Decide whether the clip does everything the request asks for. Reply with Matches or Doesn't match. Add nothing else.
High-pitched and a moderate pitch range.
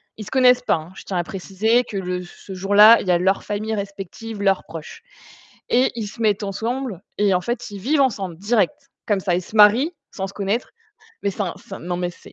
Matches